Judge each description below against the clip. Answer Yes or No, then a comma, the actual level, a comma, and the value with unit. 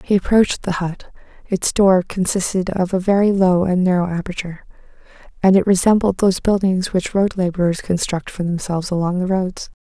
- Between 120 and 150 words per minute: No, average, 170 wpm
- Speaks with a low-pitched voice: No, medium, 185 Hz